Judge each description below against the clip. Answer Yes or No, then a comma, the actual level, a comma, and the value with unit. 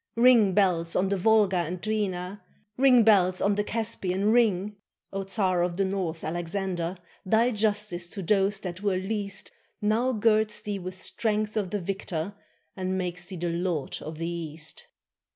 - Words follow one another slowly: No, average, 165 wpm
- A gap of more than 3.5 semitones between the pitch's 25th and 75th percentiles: No, average, 3.0 semitones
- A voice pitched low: No, high, 195 Hz